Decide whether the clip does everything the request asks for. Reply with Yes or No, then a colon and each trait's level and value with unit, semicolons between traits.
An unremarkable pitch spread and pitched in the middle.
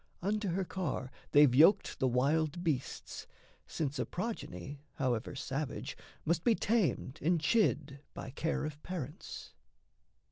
Yes: average, 5.0 semitones; medium, 155 Hz